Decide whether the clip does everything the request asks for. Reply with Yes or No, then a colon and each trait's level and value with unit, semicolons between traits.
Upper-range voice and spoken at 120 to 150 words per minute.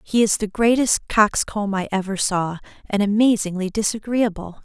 Yes: high, 205 Hz; average, 140 wpm